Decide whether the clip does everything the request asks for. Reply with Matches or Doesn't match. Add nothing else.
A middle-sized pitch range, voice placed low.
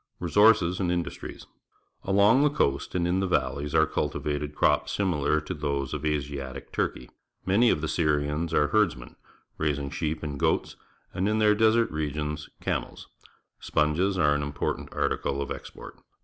Matches